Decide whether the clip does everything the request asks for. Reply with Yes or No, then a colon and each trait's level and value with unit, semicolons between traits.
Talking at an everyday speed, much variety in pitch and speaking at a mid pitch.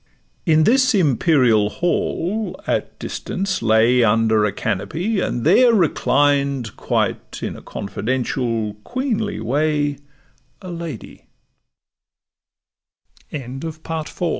No: slow, 100 wpm; wide, 7.4 semitones; medium, 145 Hz